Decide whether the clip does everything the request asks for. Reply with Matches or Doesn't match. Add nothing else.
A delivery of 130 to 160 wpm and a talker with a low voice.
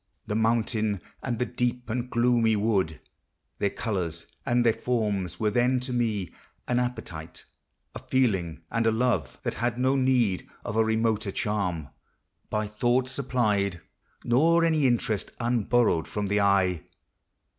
Matches